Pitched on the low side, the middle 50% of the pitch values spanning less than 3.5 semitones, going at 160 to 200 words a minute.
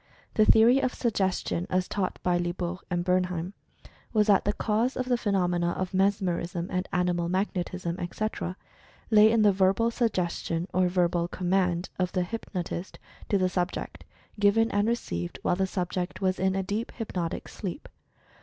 No: medium, 185 Hz; average, 2.7 semitones; average, 165 wpm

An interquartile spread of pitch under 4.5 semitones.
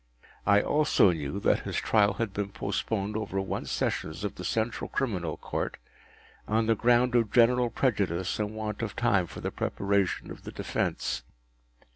Yes: average, 3.0 semitones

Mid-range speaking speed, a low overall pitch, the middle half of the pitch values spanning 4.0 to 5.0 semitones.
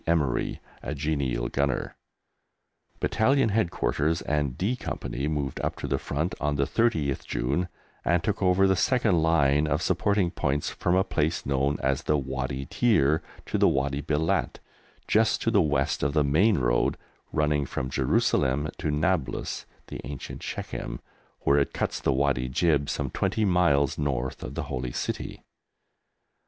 Yes: average, 155 wpm; very low, 75 Hz; average, 4.3 semitones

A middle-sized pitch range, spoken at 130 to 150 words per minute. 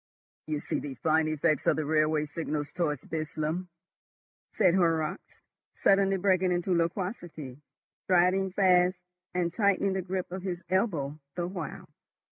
Yes: average, 3.2 semitones; slow, 135 wpm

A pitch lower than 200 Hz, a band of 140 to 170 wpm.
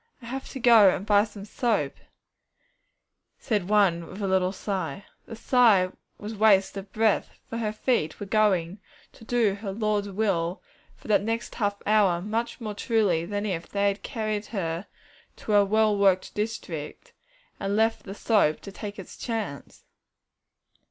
No: high, 205 Hz; average, 165 wpm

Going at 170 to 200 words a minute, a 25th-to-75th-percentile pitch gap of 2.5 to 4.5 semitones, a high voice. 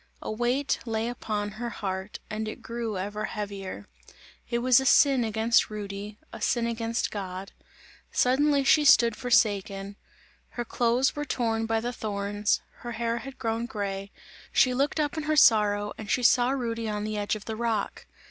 Yes: average, 175 wpm; average, 2.8 semitones; high, 225 Hz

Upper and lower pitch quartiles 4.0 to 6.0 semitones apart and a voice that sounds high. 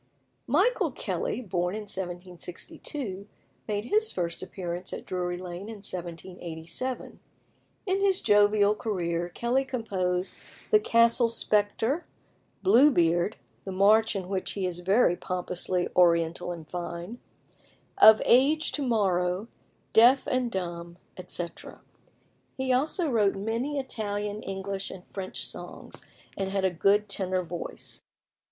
Yes: average, 4.6 semitones; high, 195 Hz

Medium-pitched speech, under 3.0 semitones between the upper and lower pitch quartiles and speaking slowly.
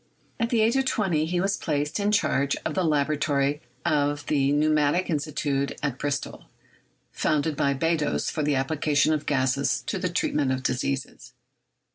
No: medium, 150 Hz; narrow, 2.5 semitones; average, 160 wpm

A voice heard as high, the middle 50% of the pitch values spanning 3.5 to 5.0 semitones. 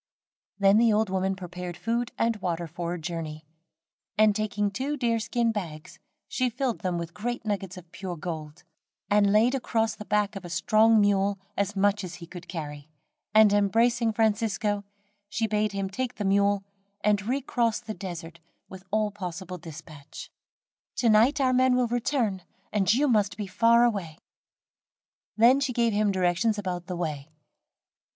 Yes: high, 205 Hz; average, 3.9 semitones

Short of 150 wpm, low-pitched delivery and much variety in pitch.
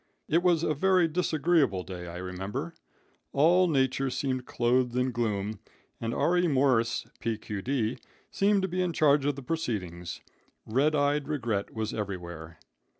Yes: average, 140 wpm; low, 130 Hz; wide, 6.7 semitones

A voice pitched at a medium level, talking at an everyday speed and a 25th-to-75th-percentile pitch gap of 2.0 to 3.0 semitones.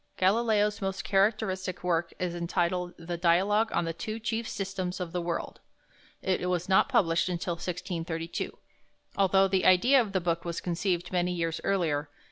Yes: medium, 180 Hz; average, 160 wpm; narrow, 2.4 semitones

